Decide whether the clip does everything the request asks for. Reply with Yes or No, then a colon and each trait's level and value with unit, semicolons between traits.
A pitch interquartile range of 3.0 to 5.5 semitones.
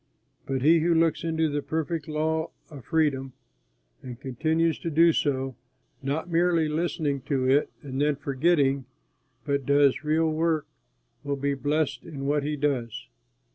No: narrow, 2.6 semitones